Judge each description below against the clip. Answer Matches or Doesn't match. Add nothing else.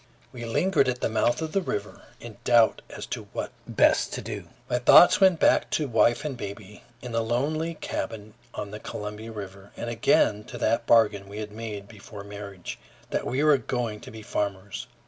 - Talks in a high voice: Doesn't match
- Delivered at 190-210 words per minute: Matches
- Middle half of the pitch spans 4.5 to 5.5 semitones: Doesn't match